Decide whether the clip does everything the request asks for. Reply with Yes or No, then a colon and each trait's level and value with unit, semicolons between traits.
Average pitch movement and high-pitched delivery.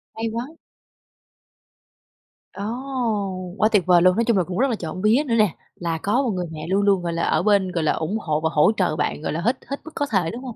Yes: average, 4.9 semitones; high, 195 Hz